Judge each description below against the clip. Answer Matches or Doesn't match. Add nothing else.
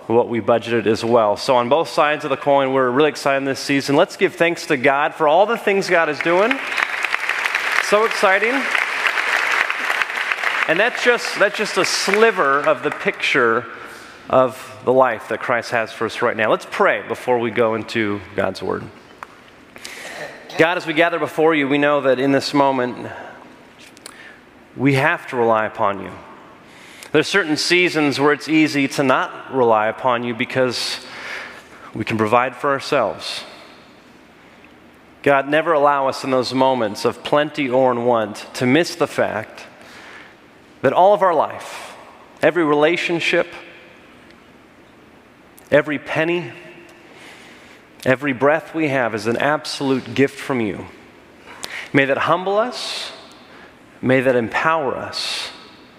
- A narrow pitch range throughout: Doesn't match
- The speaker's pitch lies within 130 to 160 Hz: Matches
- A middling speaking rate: Matches